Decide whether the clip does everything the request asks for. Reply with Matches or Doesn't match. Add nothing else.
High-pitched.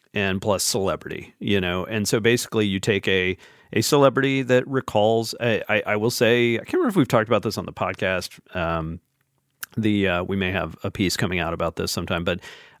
Doesn't match